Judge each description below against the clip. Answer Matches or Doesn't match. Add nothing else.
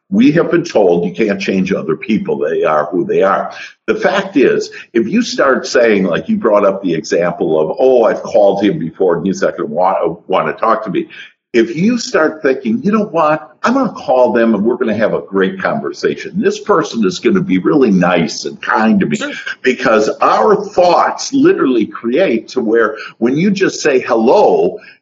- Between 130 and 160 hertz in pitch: Doesn't match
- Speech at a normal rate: Doesn't match